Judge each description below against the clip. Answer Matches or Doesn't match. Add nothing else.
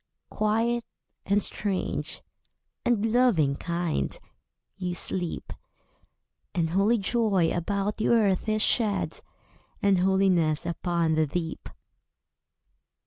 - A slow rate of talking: Matches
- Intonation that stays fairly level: Doesn't match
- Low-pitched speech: Doesn't match